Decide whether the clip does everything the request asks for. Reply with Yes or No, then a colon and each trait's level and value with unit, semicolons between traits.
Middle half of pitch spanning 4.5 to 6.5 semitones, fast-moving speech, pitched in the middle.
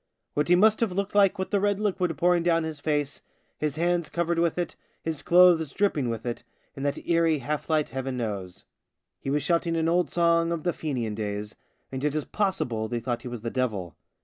Yes: wide, 5.4 semitones; fast, 215 wpm; medium, 160 Hz